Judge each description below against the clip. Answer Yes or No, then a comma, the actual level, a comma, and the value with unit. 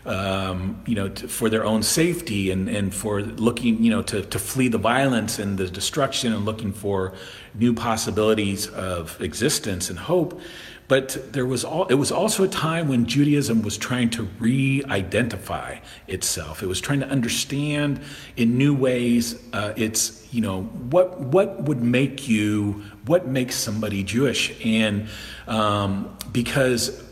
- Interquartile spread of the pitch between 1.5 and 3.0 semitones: No, average, 4.4 semitones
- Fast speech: No, average, 155 wpm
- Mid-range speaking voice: No, low, 115 Hz